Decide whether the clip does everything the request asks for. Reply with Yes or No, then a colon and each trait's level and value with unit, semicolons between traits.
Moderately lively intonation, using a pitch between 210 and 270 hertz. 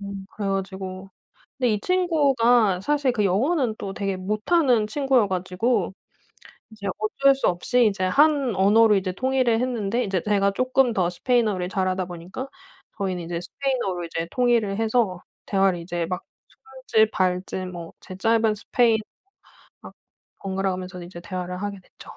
No: average, 4.7 semitones; high, 200 Hz